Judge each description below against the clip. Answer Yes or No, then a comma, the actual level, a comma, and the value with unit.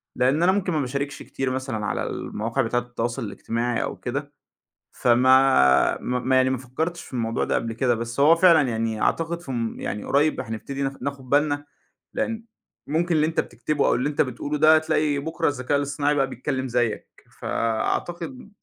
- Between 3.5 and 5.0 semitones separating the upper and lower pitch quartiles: Yes, average, 3.8 semitones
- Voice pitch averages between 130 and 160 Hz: Yes, low, 135 Hz